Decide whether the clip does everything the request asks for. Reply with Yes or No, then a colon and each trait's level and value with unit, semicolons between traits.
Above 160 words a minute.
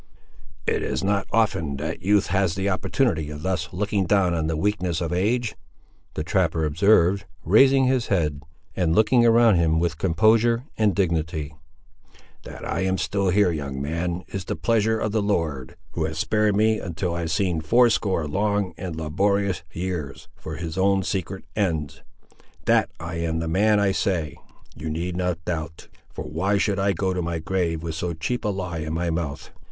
Yes: average, 180 wpm